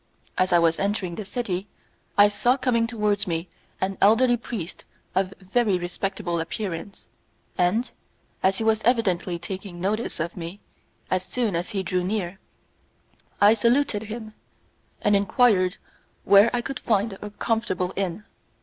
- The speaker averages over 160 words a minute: No, average, 145 wpm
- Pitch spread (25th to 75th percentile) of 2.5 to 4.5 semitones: Yes, average, 3.4 semitones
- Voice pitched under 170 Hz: No, high, 200 Hz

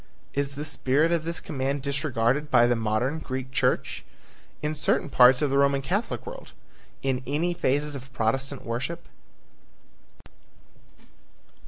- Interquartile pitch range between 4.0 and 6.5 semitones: No, average, 2.7 semitones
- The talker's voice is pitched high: No, medium, 140 Hz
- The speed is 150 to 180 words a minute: No, slow, 135 wpm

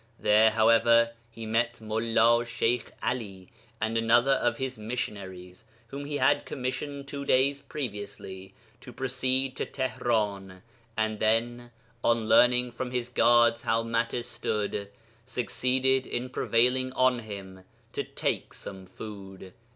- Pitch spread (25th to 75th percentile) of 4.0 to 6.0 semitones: No, average, 2.8 semitones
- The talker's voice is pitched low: Yes, low, 115 Hz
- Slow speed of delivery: Yes, slow, 130 wpm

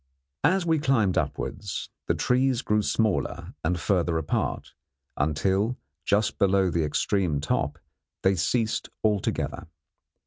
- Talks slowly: Yes, slow, 115 wpm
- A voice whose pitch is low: Yes, low, 100 Hz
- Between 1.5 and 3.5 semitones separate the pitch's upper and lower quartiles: No, average, 4.7 semitones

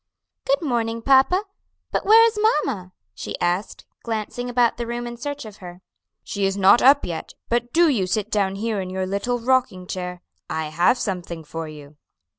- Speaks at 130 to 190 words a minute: Yes, average, 185 wpm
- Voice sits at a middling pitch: No, high, 215 Hz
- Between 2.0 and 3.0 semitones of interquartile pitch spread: No, average, 5.2 semitones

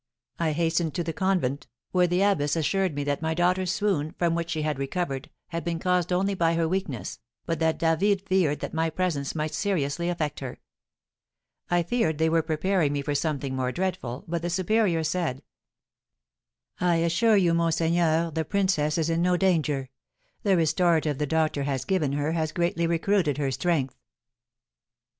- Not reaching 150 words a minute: No, average, 175 wpm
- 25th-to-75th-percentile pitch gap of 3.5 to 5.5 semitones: No, average, 3.0 semitones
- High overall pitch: No, medium, 165 Hz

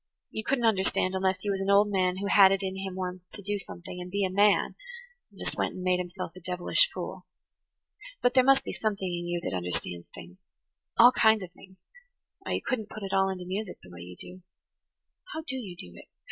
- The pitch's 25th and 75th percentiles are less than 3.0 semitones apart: Yes, narrow, 2.5 semitones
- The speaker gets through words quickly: Yes, fast, 220 wpm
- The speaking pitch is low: No, high, 190 Hz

